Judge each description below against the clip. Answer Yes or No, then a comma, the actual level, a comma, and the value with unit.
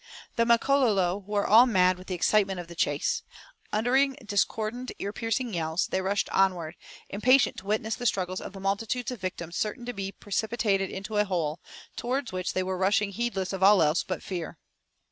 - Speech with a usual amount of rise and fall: Yes, average, 3.5 semitones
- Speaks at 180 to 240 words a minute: Yes, average, 185 wpm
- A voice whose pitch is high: Yes, high, 200 Hz